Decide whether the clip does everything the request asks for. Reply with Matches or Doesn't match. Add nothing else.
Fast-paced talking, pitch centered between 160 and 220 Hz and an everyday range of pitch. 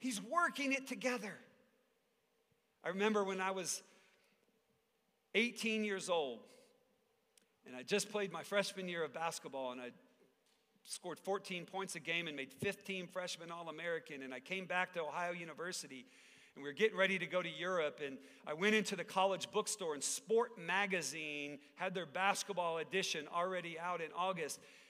Doesn't match